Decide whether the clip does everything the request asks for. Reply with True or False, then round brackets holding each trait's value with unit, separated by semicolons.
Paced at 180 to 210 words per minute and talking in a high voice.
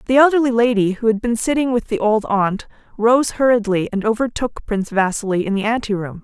True (190 wpm; 225 Hz)